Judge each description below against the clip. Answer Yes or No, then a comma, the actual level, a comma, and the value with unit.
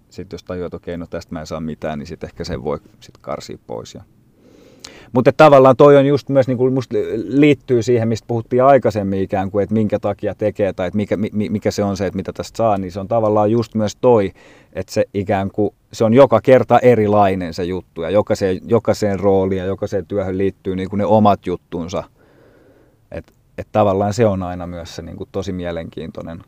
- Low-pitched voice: Yes, low, 105 Hz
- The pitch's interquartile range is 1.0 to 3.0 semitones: No, average, 3.6 semitones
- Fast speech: Yes, fast, 200 wpm